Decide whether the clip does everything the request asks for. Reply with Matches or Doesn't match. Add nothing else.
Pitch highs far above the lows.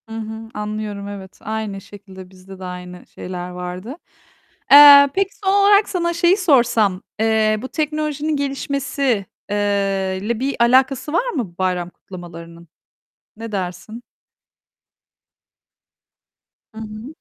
Matches